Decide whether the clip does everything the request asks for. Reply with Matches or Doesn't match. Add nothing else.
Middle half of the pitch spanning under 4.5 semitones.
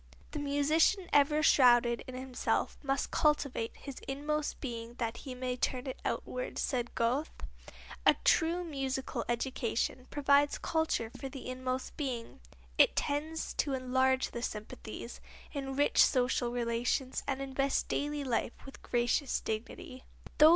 Matches